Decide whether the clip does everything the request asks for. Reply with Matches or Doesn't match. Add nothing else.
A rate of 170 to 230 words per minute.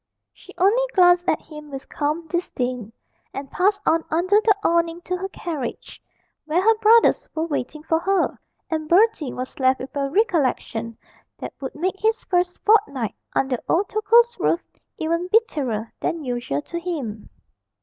Doesn't match